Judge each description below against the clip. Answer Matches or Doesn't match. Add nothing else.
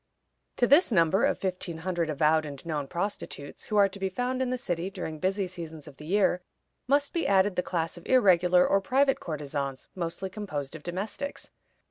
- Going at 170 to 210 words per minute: Matches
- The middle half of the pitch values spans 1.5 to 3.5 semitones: Doesn't match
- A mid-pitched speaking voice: Matches